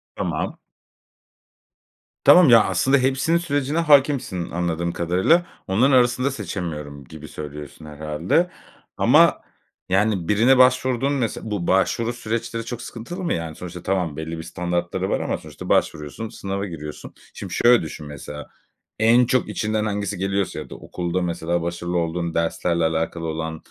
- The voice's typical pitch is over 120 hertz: No, very low, 95 Hz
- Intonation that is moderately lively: No, wide, 6.6 semitones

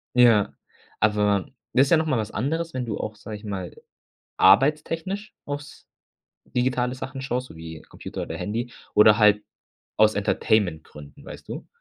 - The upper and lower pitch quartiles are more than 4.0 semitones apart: Yes, average, 4.5 semitones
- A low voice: Yes, low, 110 Hz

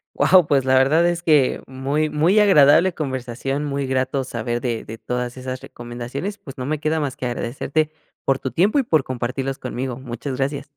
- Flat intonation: No, average, 3.2 semitones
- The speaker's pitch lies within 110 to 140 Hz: Yes, low, 135 Hz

